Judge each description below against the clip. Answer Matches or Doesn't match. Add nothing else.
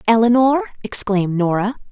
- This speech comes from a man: Doesn't match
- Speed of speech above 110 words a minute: Doesn't match